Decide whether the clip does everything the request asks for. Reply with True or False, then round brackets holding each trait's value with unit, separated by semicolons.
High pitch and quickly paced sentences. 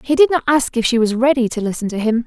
True (245 Hz; 320 wpm)